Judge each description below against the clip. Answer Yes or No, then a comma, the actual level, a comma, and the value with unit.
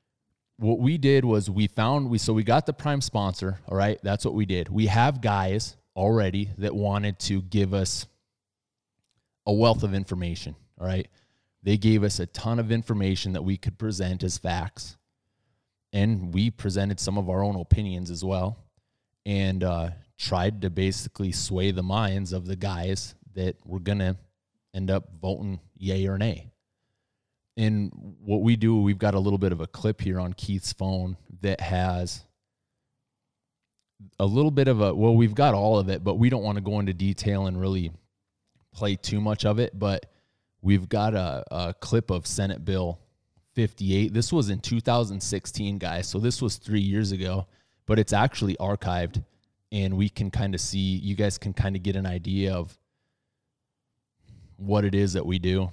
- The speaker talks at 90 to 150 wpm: No, average, 180 wpm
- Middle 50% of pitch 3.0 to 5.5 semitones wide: No, narrow, 2.6 semitones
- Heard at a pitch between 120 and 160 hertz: No, low, 100 Hz